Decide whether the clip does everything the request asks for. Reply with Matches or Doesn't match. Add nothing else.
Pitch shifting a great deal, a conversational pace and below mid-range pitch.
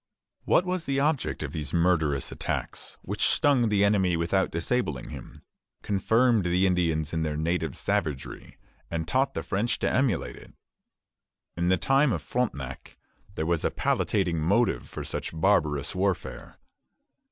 Matches